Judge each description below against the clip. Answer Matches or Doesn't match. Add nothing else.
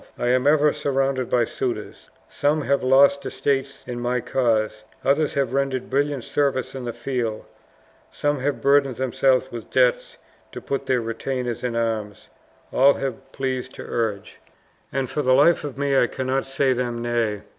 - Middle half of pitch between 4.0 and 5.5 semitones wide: Doesn't match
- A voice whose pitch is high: Doesn't match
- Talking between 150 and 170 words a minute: Matches